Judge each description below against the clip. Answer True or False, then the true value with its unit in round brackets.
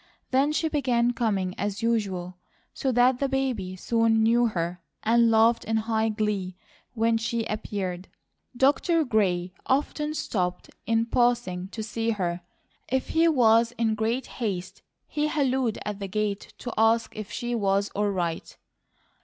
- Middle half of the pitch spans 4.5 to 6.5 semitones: False (3.5 semitones)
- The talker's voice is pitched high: True (225 Hz)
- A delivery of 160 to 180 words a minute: False (150 wpm)